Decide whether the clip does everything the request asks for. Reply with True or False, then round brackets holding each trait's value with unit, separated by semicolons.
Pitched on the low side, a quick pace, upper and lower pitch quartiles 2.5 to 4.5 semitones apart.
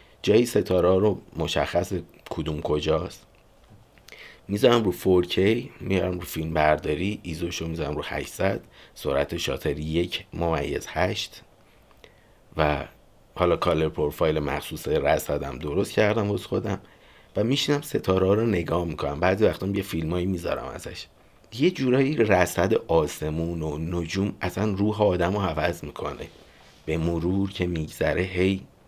False (90 Hz; 130 wpm; 3.8 semitones)